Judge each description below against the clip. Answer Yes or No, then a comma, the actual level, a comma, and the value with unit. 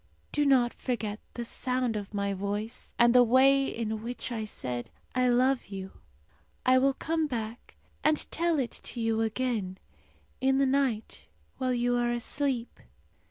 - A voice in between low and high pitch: No, high, 240 Hz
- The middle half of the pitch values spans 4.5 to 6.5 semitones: No, average, 3.0 semitones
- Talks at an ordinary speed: Yes, average, 160 wpm